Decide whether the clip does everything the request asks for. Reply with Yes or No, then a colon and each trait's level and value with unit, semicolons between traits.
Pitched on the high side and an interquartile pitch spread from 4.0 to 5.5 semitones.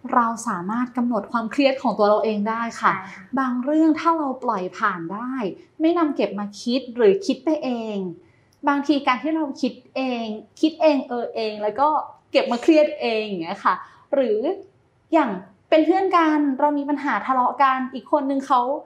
Yes: very high, 260 Hz; average, 4.9 semitones